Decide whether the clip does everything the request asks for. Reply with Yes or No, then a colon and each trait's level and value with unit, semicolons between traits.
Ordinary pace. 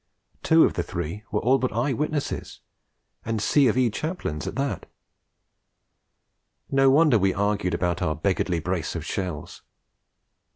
Yes: average, 150 wpm